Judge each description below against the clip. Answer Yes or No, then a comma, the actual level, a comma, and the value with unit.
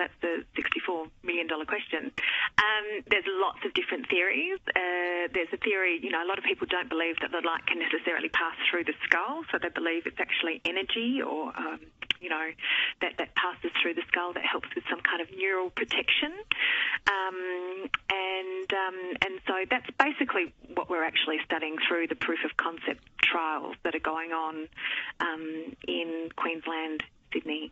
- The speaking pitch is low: No, medium, 180 Hz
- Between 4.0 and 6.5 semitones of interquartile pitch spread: Yes, average, 5.2 semitones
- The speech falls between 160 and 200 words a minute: Yes, average, 175 wpm